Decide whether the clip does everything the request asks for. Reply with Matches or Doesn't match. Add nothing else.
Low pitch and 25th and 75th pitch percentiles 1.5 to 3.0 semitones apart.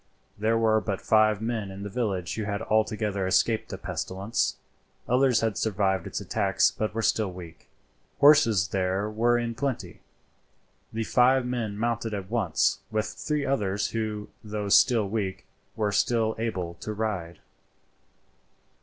Matches